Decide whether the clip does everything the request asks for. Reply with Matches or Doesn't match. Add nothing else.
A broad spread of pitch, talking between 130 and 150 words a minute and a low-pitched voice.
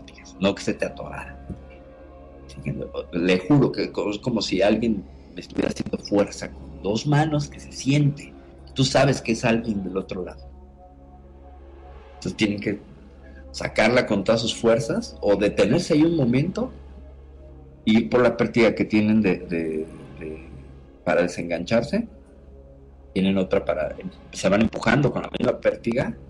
Matches